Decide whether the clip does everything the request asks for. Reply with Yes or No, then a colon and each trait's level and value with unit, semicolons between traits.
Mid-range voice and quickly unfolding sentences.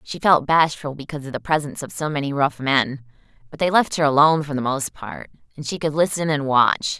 Yes: medium, 145 Hz; fast, 230 wpm